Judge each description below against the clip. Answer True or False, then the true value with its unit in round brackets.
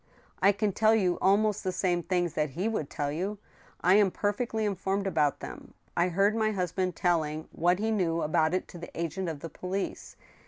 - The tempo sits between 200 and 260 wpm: True (205 wpm)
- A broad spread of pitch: False (3.3 semitones)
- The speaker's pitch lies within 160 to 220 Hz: True (185 Hz)